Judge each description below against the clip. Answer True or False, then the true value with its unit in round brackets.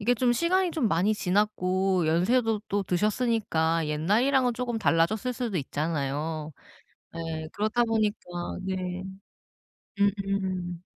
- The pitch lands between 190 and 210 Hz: True (195 Hz)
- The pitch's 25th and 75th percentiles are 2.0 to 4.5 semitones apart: False (5.2 semitones)